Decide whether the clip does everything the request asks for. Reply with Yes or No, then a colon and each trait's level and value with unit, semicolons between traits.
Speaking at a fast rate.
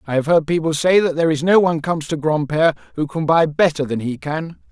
Yes: fast, 255 wpm